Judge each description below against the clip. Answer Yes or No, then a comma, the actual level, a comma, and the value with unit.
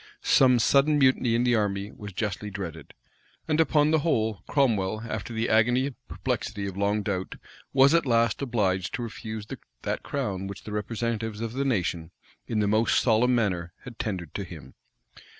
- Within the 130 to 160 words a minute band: No, average, 175 wpm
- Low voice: Yes, low, 110 Hz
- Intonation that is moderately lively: Yes, average, 3.9 semitones